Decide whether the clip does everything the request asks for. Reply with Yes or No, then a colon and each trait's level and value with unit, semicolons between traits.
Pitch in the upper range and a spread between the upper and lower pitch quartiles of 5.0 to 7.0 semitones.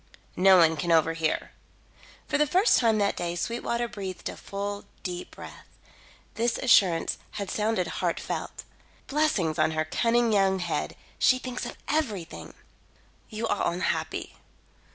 Yes: high, 200 Hz; average, 5.3 semitones